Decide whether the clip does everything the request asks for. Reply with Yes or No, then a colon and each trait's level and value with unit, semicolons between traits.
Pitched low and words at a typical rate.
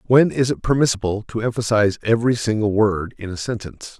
Yes: low, 110 Hz; average, 180 wpm